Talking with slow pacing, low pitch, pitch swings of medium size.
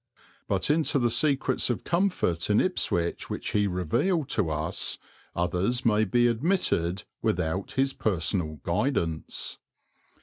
No: slow, 125 wpm; low, 105 Hz; wide, 7.6 semitones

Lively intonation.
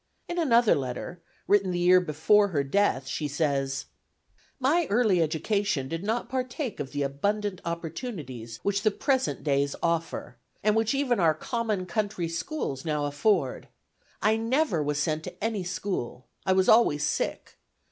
Yes: wide, 6.7 semitones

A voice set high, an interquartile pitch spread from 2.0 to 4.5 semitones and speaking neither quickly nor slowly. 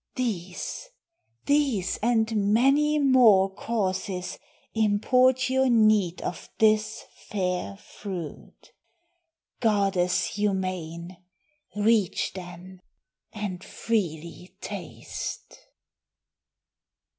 No: high, 205 Hz; average, 3.9 semitones; slow, 70 wpm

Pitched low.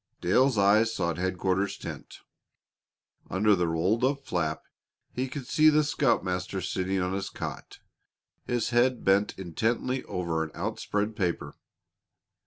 Yes: low, 100 Hz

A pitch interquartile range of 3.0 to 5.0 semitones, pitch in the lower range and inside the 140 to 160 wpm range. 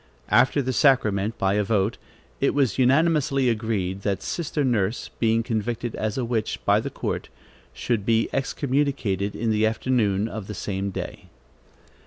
Yes: average, 4.1 semitones; low, 115 Hz; average, 155 wpm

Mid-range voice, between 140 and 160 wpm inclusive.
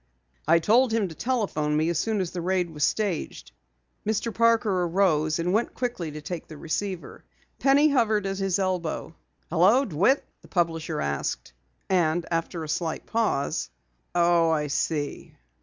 Yes: medium, 175 Hz; average, 155 wpm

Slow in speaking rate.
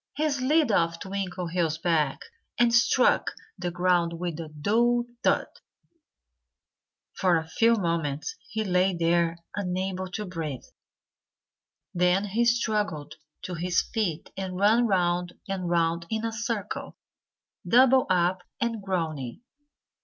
Yes: slow, 125 wpm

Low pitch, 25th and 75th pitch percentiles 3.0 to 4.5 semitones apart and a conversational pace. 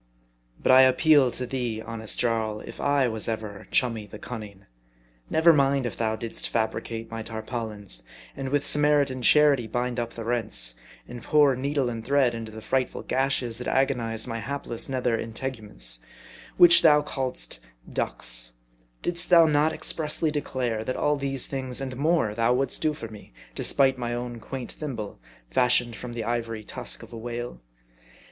Yes: low, 120 Hz; average, 3.5 semitones; average, 170 wpm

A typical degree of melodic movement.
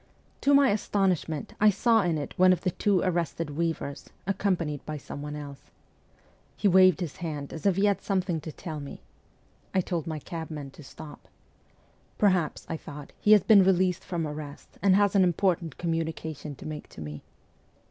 Yes: average, 3.9 semitones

